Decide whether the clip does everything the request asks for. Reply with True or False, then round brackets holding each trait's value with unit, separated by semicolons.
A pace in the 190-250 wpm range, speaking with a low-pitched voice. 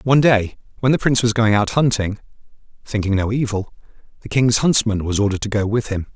True (205 wpm; 110 Hz)